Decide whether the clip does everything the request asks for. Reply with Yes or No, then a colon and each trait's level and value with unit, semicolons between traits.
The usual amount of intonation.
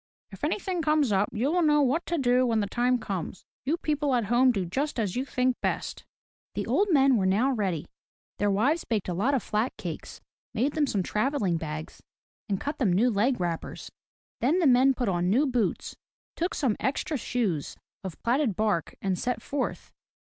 No: wide, 5.8 semitones